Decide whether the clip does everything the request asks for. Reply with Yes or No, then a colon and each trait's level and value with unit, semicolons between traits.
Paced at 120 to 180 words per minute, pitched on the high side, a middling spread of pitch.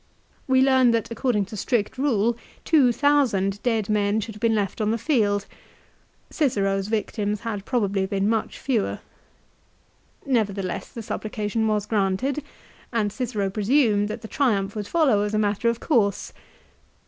Yes: average, 155 wpm; high, 215 Hz; average, 3.0 semitones